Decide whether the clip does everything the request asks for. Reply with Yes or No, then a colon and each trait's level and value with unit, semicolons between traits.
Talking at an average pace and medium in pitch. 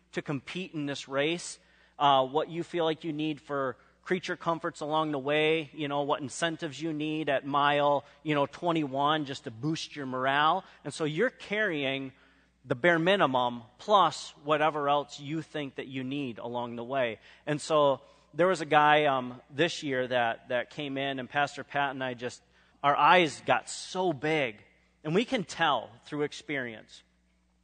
Yes: average, 180 wpm; medium, 145 Hz